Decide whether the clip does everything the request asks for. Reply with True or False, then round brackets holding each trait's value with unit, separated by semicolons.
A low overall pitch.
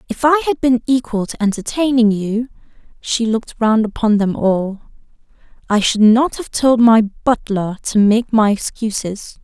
False (225 Hz)